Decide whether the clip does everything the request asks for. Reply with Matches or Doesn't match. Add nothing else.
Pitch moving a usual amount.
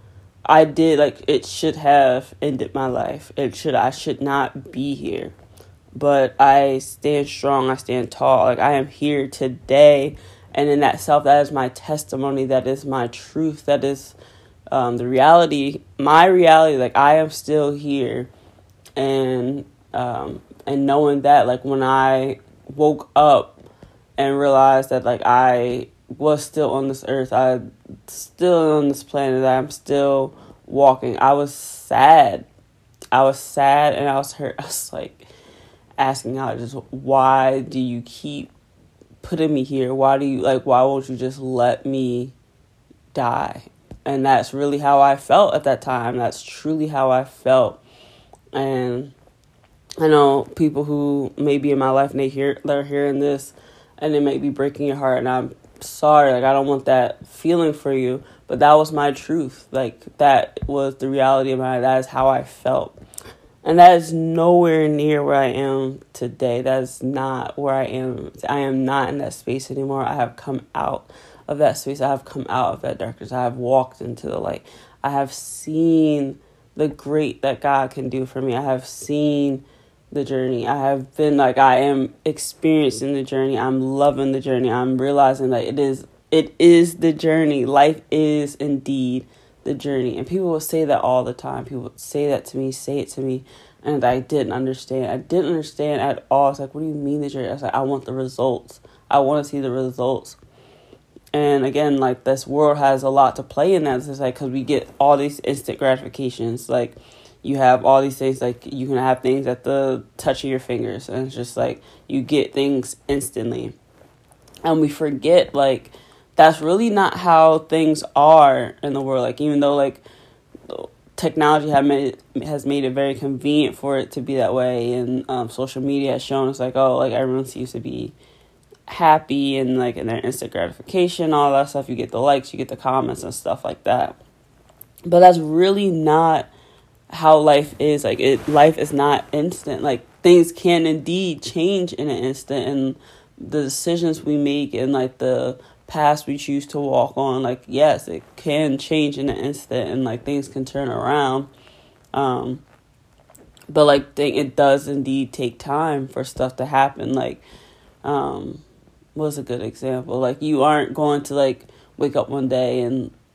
Doesn't match